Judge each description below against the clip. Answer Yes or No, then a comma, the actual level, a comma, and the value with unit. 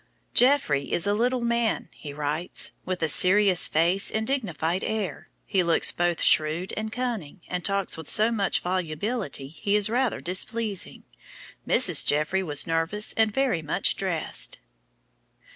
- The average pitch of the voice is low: No, high, 190 Hz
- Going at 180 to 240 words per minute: No, average, 145 wpm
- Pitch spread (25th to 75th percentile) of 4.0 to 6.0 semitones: Yes, average, 5.2 semitones